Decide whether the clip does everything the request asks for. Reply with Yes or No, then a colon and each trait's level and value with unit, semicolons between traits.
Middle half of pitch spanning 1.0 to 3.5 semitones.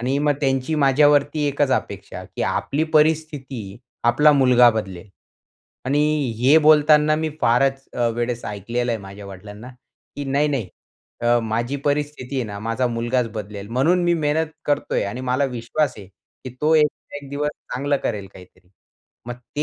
No: average, 3.9 semitones